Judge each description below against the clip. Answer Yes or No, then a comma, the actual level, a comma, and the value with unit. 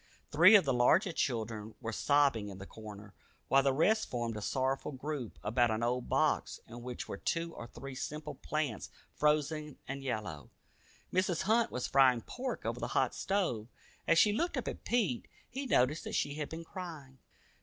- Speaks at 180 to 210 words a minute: Yes, average, 185 wpm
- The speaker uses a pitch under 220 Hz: Yes, low, 135 Hz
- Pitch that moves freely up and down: Yes, wide, 5.7 semitones